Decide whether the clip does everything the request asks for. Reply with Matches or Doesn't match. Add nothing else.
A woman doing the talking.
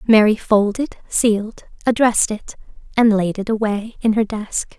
Matches